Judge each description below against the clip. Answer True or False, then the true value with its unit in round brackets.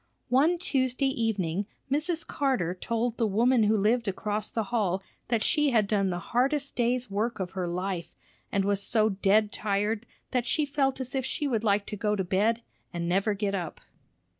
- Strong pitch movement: False (4.1 semitones)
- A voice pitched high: True (215 Hz)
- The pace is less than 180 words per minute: False (190 wpm)